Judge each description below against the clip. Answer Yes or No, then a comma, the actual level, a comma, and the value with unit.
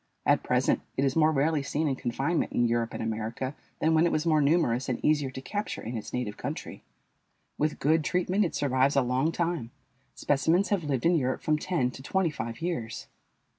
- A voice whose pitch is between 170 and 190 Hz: No, medium, 145 Hz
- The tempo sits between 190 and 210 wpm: Yes, fast, 205 wpm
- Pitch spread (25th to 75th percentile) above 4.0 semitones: Yes, average, 4.5 semitones